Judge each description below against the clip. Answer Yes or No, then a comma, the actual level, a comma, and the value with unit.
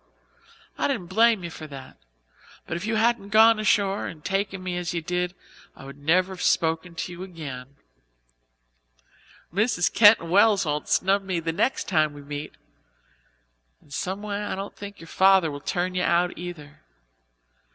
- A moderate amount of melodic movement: Yes, average, 3.8 semitones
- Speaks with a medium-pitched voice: Yes, medium, 180 Hz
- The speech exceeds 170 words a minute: No, average, 165 wpm